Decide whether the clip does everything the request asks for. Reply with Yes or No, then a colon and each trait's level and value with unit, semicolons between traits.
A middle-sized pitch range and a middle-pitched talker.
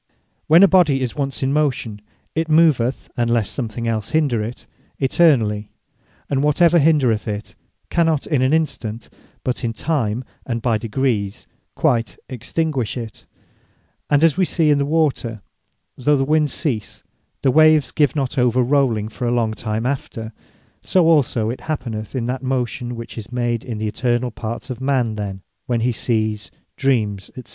No: average, 4.4 semitones; low, 125 Hz